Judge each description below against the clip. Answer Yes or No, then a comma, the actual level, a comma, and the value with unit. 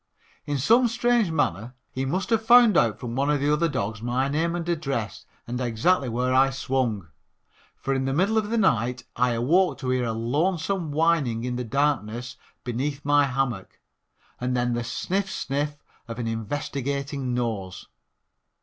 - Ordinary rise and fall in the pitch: Yes, average, 4.8 semitones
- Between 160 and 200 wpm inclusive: Yes, average, 170 wpm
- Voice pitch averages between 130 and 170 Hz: Yes, low, 135 Hz